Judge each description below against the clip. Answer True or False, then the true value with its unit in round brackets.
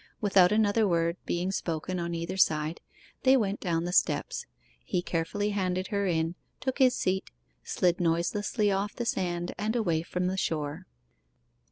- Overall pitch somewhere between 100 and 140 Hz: False (185 Hz)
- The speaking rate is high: False (160 wpm)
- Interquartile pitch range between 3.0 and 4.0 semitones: True (3.3 semitones)